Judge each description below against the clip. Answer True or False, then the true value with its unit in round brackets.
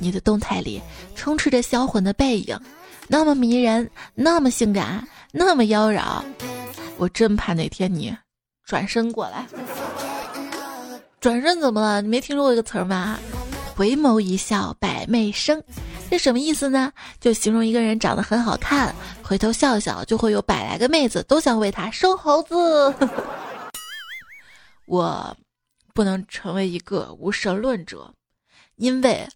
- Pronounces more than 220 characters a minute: False (215 characters per minute)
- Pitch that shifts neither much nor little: True (4.8 semitones)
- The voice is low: False (230 Hz)